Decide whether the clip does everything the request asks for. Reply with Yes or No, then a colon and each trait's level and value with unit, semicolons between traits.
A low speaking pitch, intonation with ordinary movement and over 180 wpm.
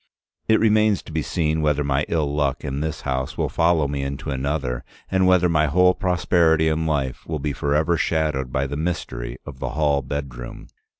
Yes: very low, 75 Hz; average, 3.0 semitones; average, 190 wpm